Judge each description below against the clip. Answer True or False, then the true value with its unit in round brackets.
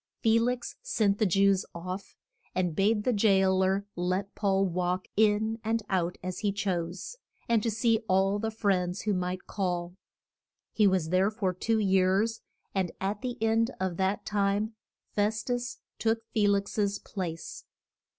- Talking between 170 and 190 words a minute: False (160 wpm)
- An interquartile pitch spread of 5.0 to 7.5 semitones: False (2.9 semitones)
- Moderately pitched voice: False (200 Hz)